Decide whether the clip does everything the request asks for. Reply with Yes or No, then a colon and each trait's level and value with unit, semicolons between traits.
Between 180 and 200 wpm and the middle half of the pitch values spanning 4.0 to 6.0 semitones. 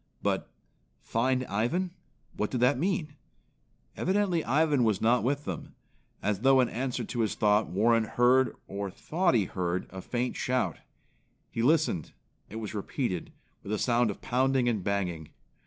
No: average, 155 wpm; average, 4.3 semitones